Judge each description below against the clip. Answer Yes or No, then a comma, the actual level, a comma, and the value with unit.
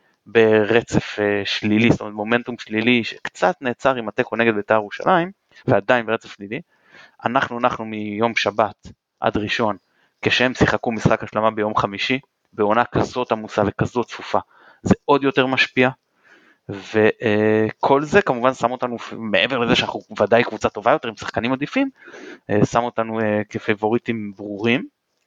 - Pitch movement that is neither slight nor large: Yes, average, 3.0 semitones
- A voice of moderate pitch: No, low, 115 Hz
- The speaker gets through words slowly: No, average, 145 wpm